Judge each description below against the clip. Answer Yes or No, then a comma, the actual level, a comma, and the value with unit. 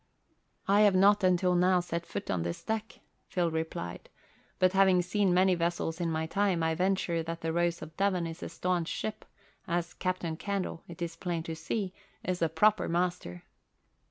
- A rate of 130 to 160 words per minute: No, average, 185 wpm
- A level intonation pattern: Yes, narrow, 2.3 semitones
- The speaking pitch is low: No, medium, 175 Hz